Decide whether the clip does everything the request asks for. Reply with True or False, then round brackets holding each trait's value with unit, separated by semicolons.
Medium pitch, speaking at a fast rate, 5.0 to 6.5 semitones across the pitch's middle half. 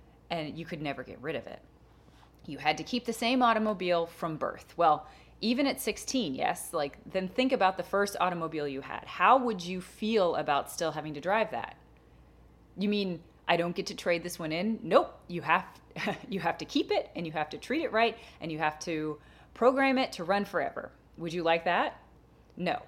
True (180 Hz; 210 wpm; 5.6 semitones)